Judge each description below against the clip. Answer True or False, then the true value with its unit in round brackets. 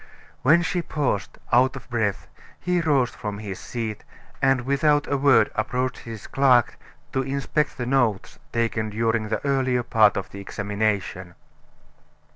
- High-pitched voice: False (120 Hz)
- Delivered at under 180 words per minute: True (145 wpm)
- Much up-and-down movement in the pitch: False (4.1 semitones)